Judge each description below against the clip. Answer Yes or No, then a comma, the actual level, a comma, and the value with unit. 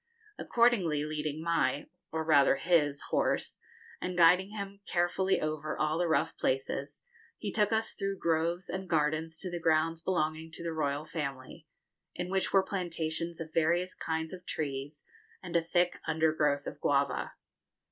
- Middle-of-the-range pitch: Yes, medium, 160 Hz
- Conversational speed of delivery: Yes, average, 155 wpm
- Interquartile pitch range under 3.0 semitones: Yes, narrow, 2.6 semitones